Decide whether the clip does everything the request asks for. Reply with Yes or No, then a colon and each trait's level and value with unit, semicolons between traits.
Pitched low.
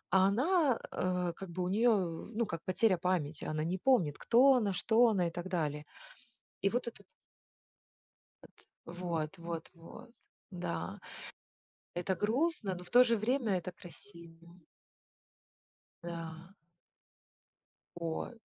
No: medium, 185 Hz